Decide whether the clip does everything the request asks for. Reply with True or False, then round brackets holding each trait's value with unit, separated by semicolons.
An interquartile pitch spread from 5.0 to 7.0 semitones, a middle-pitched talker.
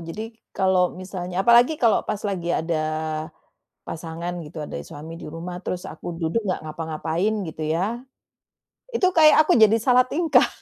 True (5.6 semitones; 180 Hz)